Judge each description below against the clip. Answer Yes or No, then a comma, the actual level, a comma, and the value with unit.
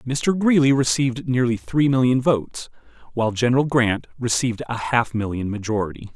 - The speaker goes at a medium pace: Yes, average, 145 wpm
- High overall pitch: No, low, 120 Hz